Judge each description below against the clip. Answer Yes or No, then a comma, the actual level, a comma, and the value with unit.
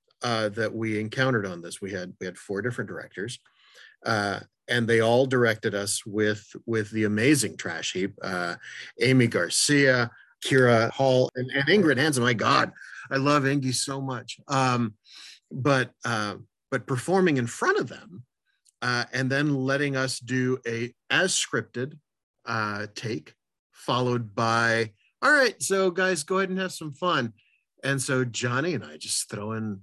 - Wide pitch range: No, average, 3.3 semitones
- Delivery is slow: No, average, 165 wpm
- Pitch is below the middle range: Yes, low, 125 Hz